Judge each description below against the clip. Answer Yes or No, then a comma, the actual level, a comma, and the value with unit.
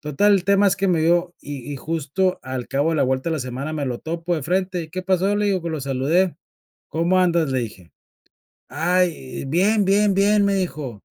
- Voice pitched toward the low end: No, medium, 170 Hz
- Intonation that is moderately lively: Yes, average, 5.0 semitones